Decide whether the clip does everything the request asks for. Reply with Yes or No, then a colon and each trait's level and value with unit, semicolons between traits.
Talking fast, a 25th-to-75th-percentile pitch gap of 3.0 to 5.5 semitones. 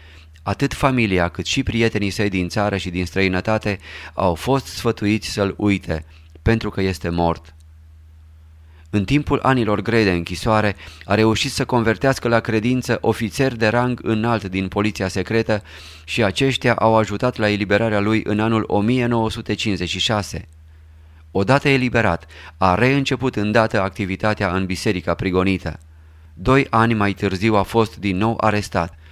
No: average, 140 wpm; average, 4.3 semitones